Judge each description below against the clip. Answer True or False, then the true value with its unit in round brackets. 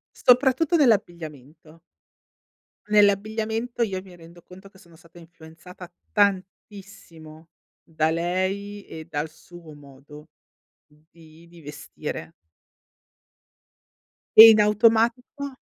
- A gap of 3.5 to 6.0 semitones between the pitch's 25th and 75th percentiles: True (4.8 semitones)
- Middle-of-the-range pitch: True (180 Hz)